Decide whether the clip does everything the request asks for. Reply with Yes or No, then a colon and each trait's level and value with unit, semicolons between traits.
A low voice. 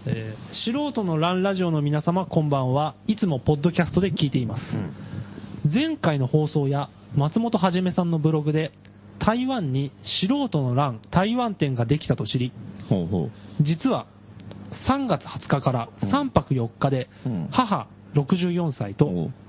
No: medium, 150 Hz